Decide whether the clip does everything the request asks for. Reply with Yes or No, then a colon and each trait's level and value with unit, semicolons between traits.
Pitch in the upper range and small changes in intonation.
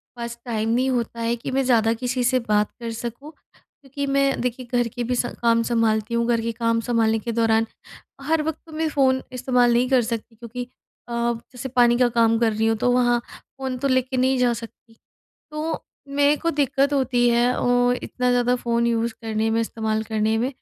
Yes: high, 240 Hz; narrow, 2.0 semitones